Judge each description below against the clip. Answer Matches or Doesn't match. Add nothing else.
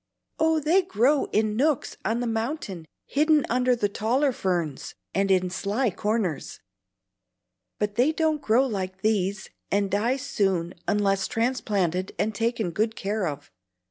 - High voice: Matches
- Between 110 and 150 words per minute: Matches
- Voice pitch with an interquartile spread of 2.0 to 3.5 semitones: Doesn't match